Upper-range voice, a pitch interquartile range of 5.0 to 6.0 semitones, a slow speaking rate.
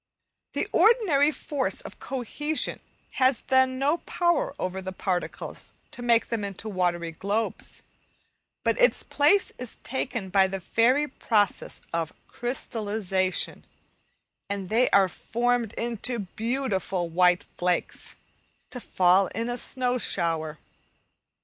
Yes: high, 225 Hz; wide, 5.5 semitones; slow, 120 wpm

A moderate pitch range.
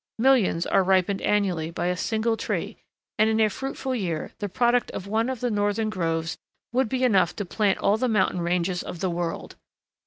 Yes: average, 4.0 semitones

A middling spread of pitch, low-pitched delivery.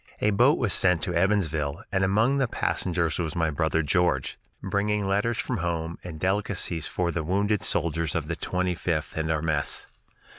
Yes: average, 3.7 semitones; very low, 90 Hz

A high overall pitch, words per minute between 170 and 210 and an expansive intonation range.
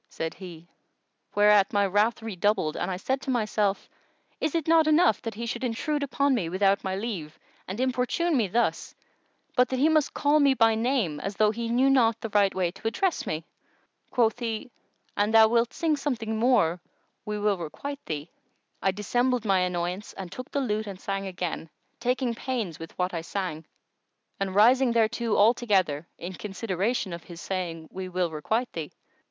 No: high, 215 Hz; average, 180 wpm; average, 4.9 semitones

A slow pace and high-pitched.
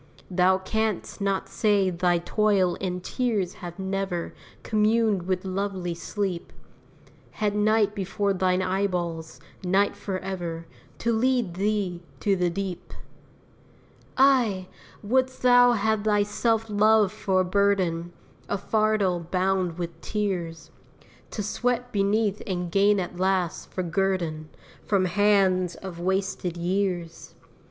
Yes: slow, 120 wpm; high, 195 Hz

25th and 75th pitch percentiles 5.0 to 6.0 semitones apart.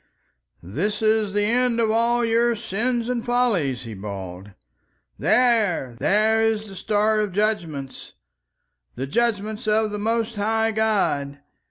No: average, 3.7 semitones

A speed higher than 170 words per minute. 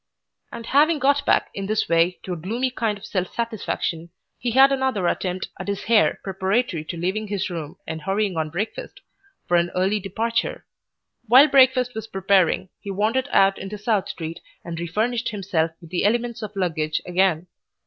Yes: average, 180 wpm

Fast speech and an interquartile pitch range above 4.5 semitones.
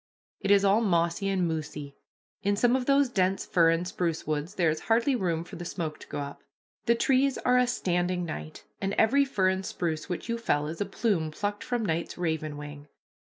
Yes: fast, 210 wpm; wide, 5.5 semitones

